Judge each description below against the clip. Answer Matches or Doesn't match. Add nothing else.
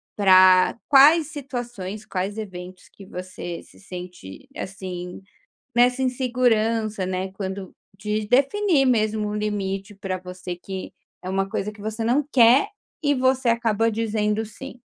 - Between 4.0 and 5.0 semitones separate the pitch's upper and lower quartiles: Matches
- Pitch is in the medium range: Doesn't match